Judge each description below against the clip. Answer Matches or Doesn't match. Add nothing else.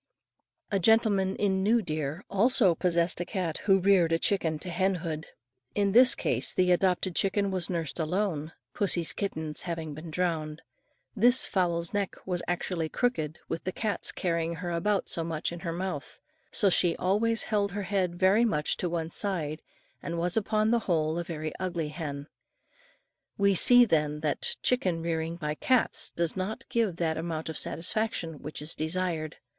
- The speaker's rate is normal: Matches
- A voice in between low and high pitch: Matches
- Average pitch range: Matches